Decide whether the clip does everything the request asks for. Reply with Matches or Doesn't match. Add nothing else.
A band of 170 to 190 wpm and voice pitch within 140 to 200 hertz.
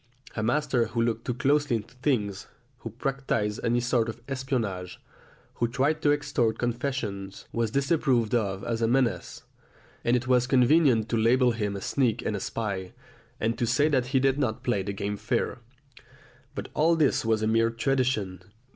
Doesn't match